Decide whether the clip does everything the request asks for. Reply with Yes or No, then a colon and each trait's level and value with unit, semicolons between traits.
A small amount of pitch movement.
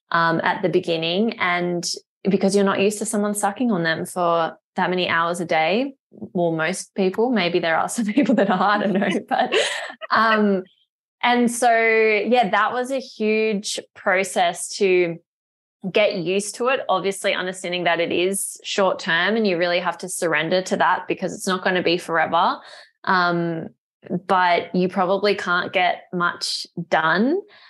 No: average, 3.6 semitones